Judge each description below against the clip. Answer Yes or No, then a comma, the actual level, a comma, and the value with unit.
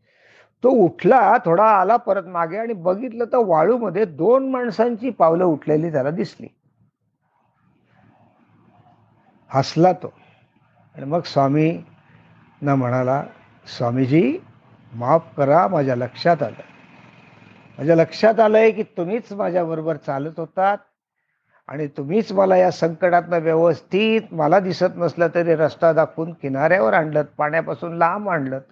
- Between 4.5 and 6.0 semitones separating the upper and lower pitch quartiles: Yes, average, 5.0 semitones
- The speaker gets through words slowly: No, average, 115 wpm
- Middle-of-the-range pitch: Yes, medium, 165 Hz